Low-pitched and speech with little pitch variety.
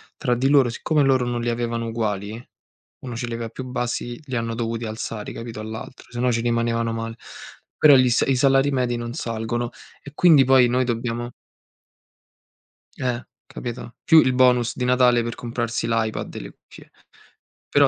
Yes: low, 120 Hz; narrow, 1.6 semitones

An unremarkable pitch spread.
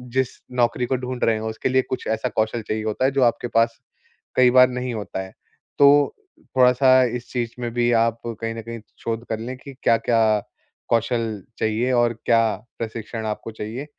No: narrow, 2.0 semitones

